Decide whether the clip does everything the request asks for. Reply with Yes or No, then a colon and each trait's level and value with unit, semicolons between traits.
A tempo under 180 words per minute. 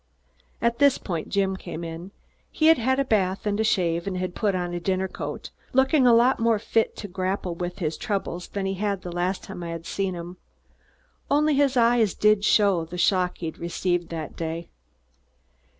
No: fast, 205 wpm